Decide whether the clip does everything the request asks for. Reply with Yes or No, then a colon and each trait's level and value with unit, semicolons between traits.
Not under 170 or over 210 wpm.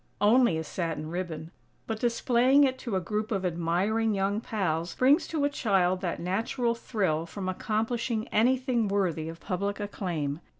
No: average, 160 wpm